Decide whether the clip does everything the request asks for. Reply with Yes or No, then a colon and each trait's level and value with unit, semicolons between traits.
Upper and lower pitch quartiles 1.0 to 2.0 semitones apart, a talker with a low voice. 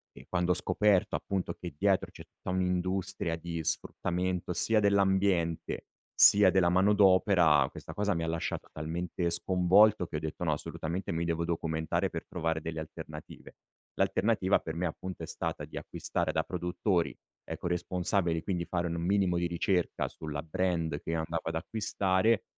No: narrow, 2.5 semitones; very low, 90 Hz